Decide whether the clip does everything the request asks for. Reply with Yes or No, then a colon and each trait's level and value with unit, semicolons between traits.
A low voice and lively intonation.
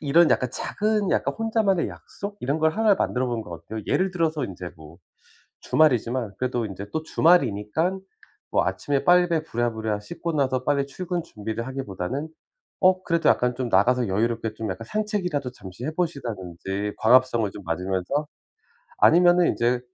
Yes: low, 130 Hz; wide, 7.5 semitones